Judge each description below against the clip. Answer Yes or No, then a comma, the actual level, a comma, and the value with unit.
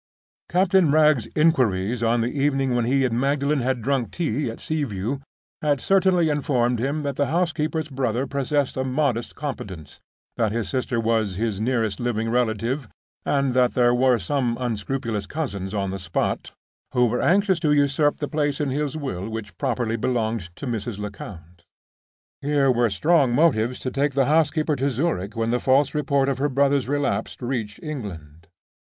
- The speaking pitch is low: Yes, low, 130 Hz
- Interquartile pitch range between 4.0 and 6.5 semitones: Yes, average, 4.3 semitones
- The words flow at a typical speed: Yes, average, 170 wpm